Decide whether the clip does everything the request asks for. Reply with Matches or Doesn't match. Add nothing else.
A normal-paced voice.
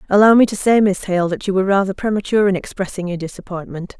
Doesn't match